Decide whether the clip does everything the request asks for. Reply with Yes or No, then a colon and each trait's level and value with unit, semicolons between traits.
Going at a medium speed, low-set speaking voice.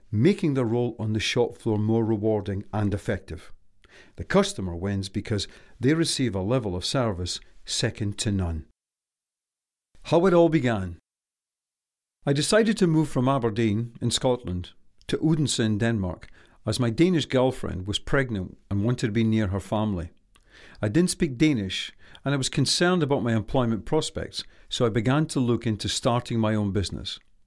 Yes: average, 165 wpm; low, 115 Hz